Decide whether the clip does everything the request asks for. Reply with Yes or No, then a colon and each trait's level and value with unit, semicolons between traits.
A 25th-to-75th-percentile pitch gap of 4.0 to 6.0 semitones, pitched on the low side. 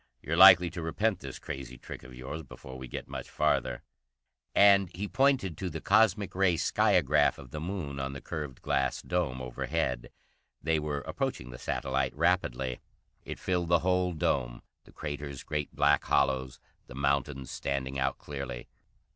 Yes: average, 5.1 semitones; very low, 75 Hz